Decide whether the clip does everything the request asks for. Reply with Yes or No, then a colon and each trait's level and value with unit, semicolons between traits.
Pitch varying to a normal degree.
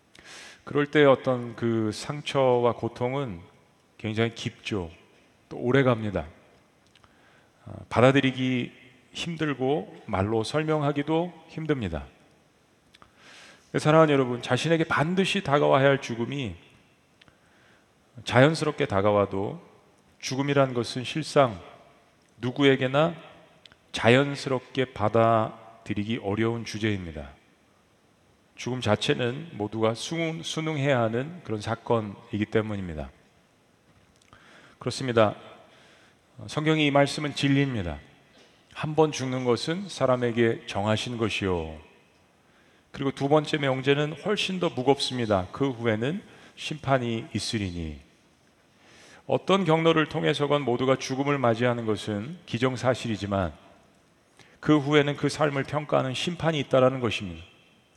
Yes: average, 4.8 semitones